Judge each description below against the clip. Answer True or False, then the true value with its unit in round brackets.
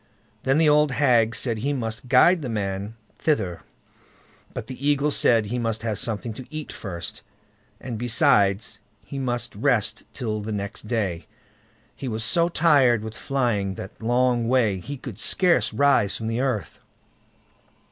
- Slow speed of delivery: False (155 wpm)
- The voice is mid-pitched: False (120 Hz)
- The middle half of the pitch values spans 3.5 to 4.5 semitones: True (4.2 semitones)